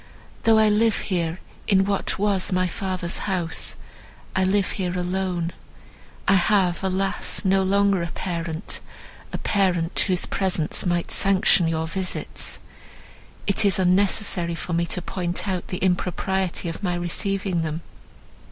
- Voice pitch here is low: No, medium, 185 Hz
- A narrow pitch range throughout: Yes, narrow, 2.0 semitones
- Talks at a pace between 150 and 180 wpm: No, slow, 135 wpm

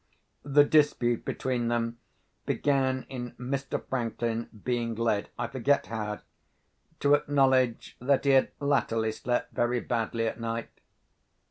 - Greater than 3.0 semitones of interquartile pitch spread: No, average, 2.7 semitones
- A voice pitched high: No, low, 120 Hz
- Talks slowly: Yes, slow, 115 wpm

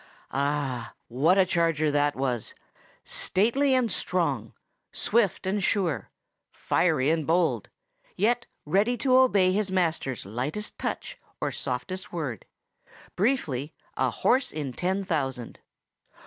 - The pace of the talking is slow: Yes, slow, 115 wpm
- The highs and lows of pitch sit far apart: Yes, wide, 6.5 semitones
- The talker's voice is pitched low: No, medium, 165 Hz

